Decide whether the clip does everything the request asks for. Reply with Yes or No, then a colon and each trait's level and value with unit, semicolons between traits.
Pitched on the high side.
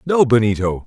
No: low, 120 Hz